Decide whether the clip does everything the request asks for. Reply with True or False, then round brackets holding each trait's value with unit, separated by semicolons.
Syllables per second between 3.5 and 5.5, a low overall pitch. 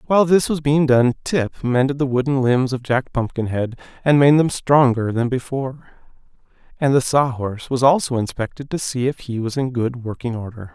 True (5.3 syllables/s; 130 Hz)